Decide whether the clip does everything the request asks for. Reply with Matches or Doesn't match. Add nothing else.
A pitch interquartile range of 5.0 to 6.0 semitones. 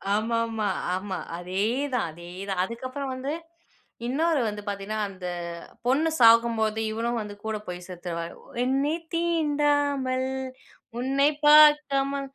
Matches